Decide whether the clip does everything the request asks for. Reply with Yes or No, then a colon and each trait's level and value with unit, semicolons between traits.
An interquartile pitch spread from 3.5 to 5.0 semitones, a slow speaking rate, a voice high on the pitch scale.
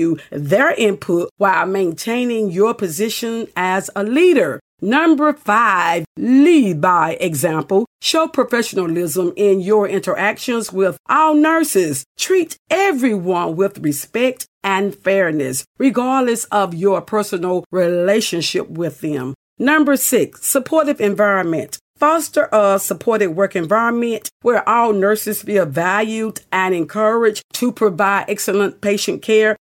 Yes: average, 4.3 semitones; slow, 115 wpm; high, 205 Hz